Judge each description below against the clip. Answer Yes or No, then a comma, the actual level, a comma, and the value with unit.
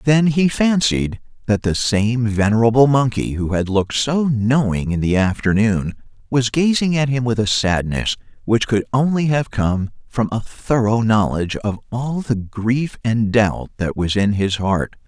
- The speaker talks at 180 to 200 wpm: No, average, 170 wpm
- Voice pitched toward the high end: No, low, 115 Hz